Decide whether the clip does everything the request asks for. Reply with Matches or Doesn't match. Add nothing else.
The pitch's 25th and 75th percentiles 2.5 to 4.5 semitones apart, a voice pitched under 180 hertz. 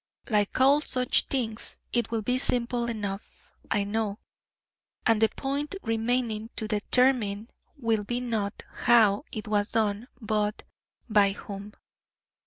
Doesn't match